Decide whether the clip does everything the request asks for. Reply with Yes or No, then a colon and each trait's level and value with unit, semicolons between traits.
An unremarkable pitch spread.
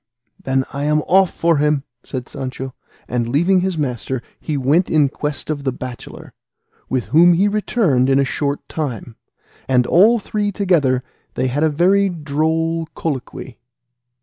Yes: average, 4.6 semitones